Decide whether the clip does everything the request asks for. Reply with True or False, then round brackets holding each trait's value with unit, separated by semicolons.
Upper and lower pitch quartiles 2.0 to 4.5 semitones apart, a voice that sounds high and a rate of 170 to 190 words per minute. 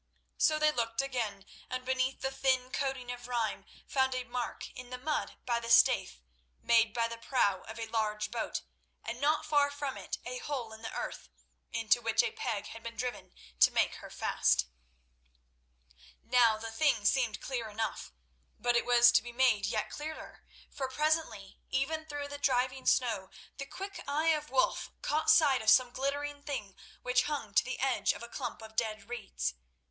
True (3.7 semitones; 250 Hz; 185 wpm)